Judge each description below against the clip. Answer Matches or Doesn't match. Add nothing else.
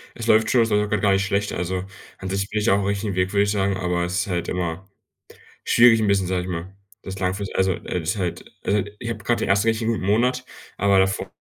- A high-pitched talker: Doesn't match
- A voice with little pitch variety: Matches